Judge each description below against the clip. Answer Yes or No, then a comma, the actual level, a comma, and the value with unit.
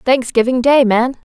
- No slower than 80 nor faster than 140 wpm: Yes, slow, 135 wpm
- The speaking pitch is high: Yes, very high, 250 Hz